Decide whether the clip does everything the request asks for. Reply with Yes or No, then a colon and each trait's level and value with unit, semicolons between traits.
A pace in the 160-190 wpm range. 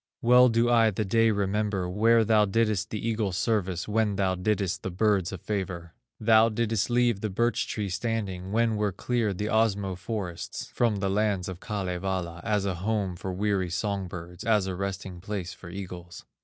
Yes: average, 185 wpm